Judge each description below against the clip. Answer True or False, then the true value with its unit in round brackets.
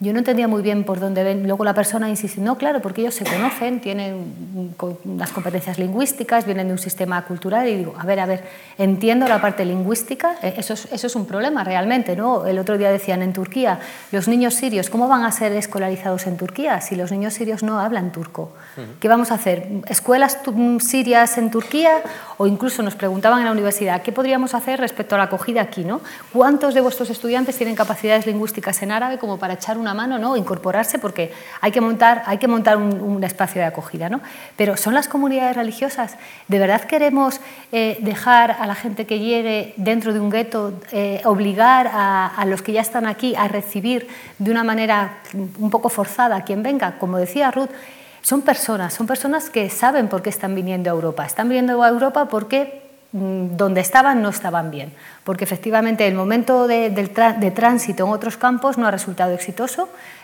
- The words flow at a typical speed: False (200 wpm)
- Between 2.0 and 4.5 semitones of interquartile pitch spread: True (3.9 semitones)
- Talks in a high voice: True (220 Hz)